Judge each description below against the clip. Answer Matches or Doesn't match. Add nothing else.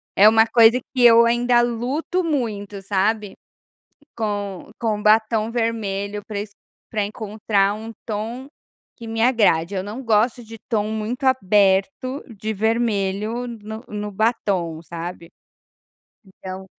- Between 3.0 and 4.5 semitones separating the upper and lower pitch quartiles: Doesn't match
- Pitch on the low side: Doesn't match